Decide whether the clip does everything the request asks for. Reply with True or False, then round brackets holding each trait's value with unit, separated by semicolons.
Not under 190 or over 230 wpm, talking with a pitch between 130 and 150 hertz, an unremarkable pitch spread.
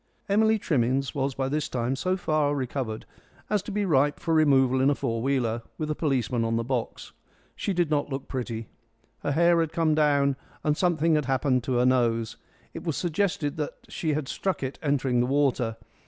True (200 wpm; 140 Hz; 3.6 semitones)